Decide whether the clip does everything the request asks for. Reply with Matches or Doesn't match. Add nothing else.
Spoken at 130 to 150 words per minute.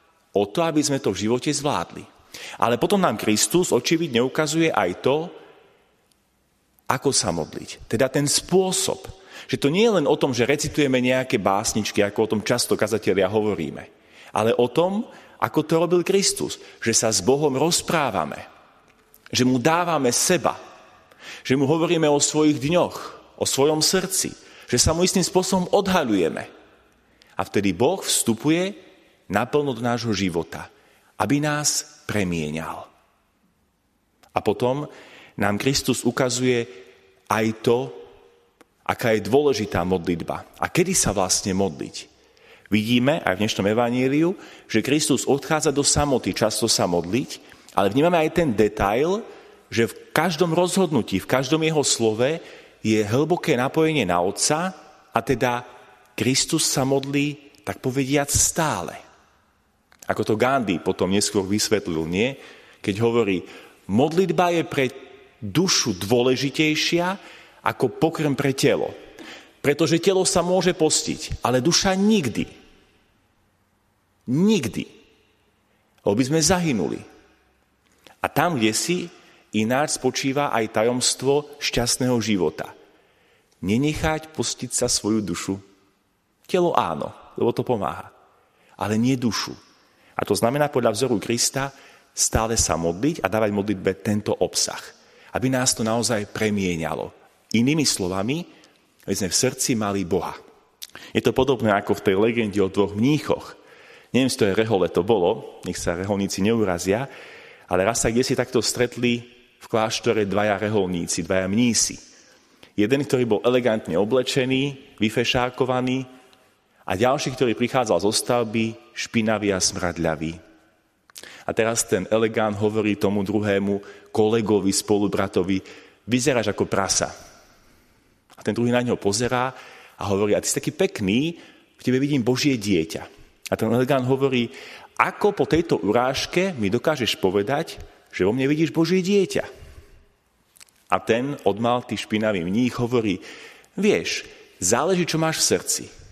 Matches